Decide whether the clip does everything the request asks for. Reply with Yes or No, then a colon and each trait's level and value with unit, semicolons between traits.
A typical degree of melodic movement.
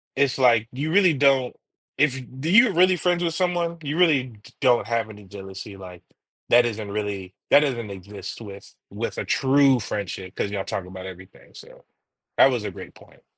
No: wide, 6.7 semitones